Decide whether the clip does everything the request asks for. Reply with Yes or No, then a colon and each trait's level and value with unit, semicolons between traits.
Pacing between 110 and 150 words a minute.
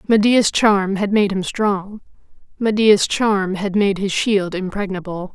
Yes: average, 145 wpm